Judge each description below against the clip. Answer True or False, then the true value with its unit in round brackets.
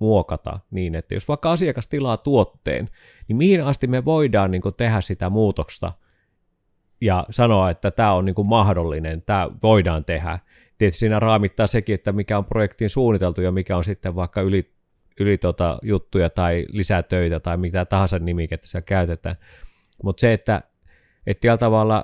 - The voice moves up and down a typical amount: True (3.5 semitones)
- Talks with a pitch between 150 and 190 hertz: False (95 Hz)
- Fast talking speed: True (165 wpm)